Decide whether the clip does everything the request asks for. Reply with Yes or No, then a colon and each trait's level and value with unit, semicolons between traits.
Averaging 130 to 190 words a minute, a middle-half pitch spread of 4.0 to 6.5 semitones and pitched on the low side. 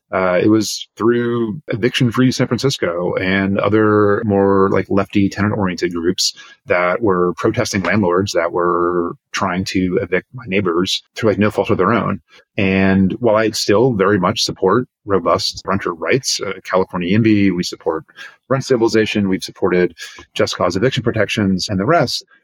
No: average, 155 wpm; average, 2.8 semitones; low, 100 Hz